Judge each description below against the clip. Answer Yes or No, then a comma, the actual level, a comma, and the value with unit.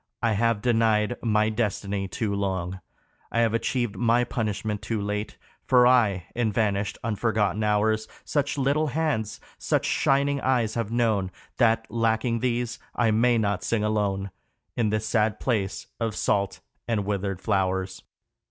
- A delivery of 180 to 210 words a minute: No, average, 145 wpm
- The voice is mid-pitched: No, low, 110 Hz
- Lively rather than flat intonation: No, narrow, 2.4 semitones